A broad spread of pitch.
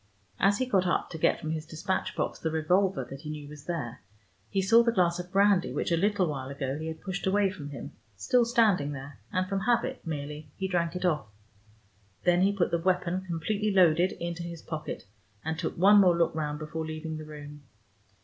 No: average, 3.8 semitones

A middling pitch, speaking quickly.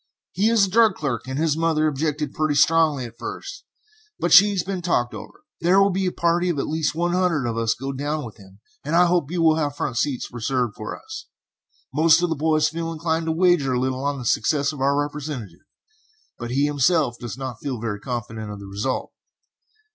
Yes: medium, 150 Hz; fast, 220 wpm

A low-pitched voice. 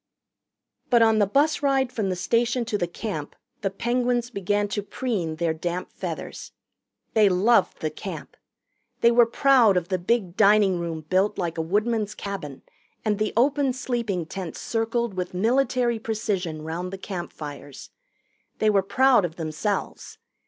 No: high, 205 Hz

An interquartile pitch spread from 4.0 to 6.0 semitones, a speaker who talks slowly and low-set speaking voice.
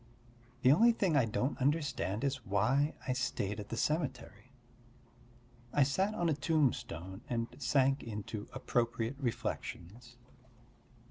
Yes: average, 4.3 semitones; slow, 125 wpm; low, 125 Hz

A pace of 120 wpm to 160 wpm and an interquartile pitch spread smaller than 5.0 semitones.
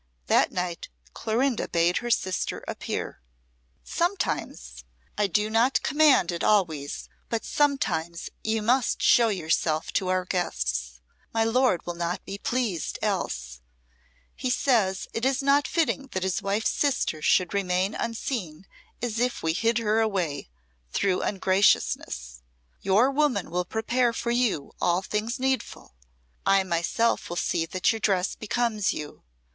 No: average, 140 wpm; wide, 5.5 semitones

